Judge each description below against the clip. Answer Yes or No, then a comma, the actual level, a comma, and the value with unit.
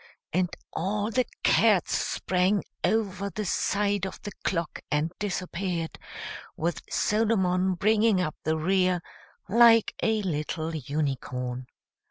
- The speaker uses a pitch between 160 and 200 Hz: Yes, medium, 185 Hz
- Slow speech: Yes, slow, 115 wpm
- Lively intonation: No, average, 4.1 semitones